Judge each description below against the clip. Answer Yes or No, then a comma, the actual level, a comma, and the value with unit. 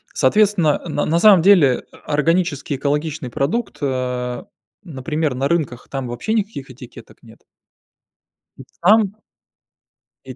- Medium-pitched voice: Yes, medium, 150 Hz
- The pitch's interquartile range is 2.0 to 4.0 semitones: No, wide, 5.6 semitones